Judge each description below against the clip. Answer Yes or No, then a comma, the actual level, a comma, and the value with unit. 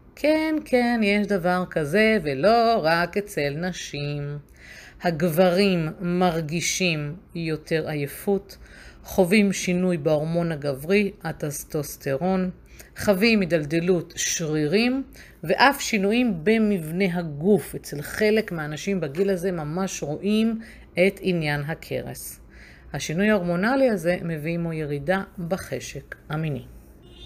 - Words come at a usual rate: No, slow, 95 wpm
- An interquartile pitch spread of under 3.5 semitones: No, average, 4.5 semitones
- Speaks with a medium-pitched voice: Yes, medium, 180 Hz